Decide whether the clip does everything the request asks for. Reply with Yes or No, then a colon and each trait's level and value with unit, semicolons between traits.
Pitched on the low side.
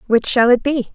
No: high, 245 Hz